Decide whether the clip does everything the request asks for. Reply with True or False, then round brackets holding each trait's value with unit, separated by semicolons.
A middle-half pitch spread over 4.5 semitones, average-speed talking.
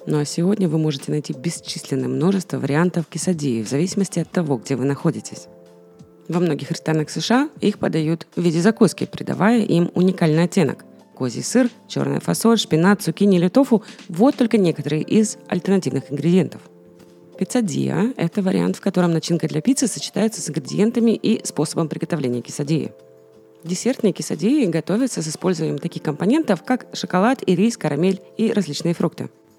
True (5.4 semitones; 150 wpm)